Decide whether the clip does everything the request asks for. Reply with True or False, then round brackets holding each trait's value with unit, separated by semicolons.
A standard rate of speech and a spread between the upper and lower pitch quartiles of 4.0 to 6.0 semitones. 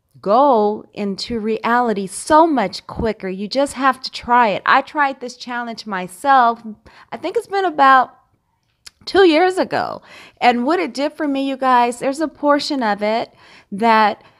True (165 wpm; 4.7 semitones)